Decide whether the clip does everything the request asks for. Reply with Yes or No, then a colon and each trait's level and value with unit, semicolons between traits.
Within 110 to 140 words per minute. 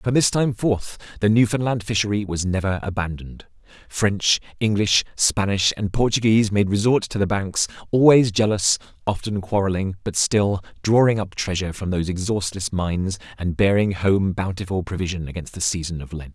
No: average, 160 wpm